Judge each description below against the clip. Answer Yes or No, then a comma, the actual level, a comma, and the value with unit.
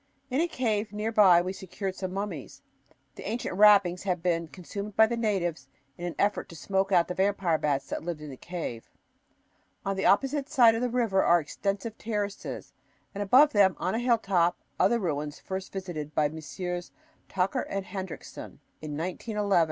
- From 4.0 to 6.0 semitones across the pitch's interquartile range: No, average, 3.4 semitones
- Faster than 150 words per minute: Yes, average, 180 wpm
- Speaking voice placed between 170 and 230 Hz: Yes, high, 190 Hz